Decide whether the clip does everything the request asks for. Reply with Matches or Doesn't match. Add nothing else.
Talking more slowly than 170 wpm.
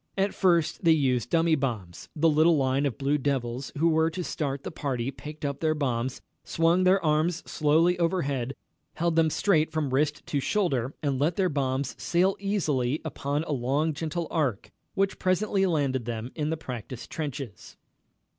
Doesn't match